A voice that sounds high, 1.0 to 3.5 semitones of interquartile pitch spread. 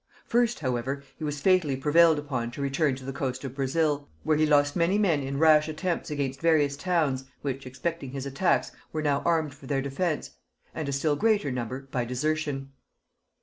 No: medium, 145 Hz; average, 2.7 semitones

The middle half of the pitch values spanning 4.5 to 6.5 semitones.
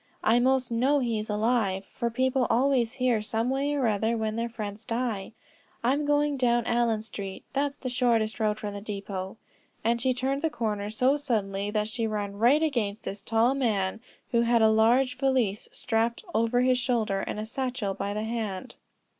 No: average, 3.1 semitones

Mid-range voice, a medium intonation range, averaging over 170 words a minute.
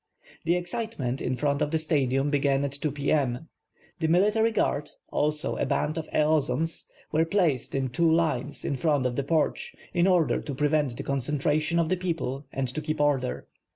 Yes: medium, 150 Hz; average, 3.0 semitones; average, 190 wpm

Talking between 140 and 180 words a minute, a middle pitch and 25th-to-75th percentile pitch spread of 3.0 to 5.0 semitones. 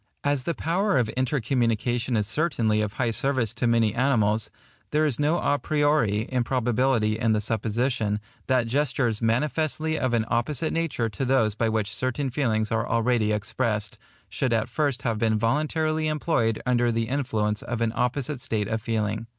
No: average, 165 wpm; low, 120 Hz; average, 3.9 semitones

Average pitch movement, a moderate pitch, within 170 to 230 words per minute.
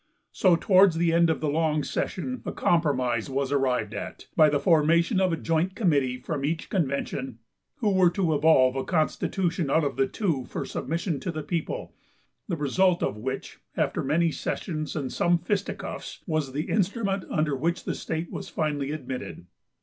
Yes: average, 3.8 semitones; medium, 160 Hz; average, 175 wpm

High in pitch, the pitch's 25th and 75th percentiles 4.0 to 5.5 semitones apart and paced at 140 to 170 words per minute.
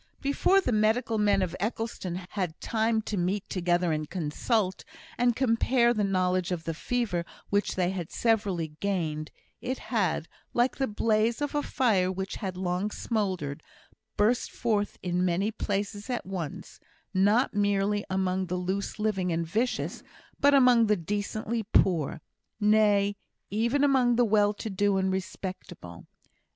No: high, 205 Hz; average, 3.6 semitones; average, 150 wpm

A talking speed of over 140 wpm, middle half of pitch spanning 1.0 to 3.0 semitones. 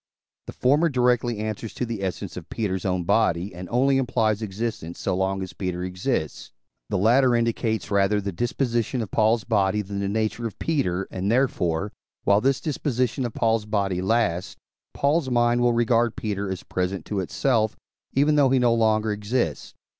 No: average, 175 wpm; average, 3.9 semitones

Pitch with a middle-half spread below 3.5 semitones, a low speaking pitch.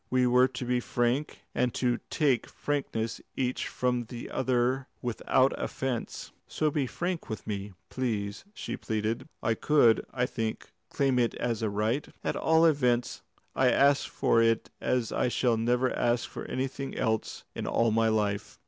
Yes: narrow, 2.6 semitones; low, 125 Hz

